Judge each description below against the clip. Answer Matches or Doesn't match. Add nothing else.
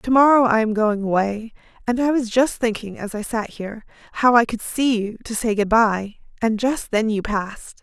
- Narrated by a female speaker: Matches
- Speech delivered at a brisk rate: Matches